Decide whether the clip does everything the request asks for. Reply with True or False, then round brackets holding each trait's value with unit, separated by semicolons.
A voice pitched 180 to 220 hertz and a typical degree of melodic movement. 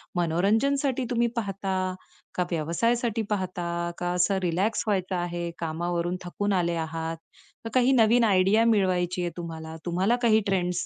True (185 Hz; 3.9 semitones)